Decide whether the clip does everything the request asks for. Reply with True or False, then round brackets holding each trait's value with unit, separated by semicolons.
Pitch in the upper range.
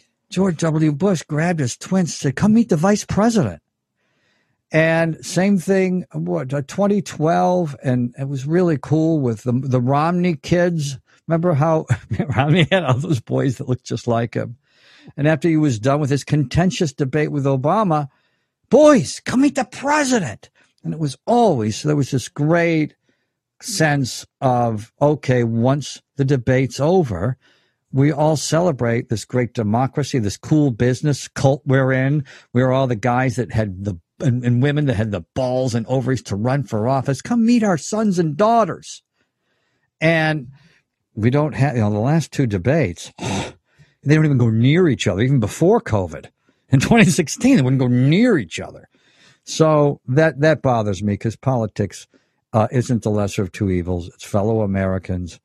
False (140 Hz)